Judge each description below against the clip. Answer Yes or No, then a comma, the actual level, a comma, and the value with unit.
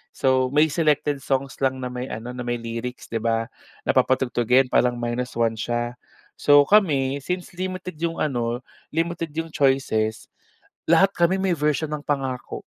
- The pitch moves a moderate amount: Yes, average, 4.4 semitones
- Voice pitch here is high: No, low, 135 Hz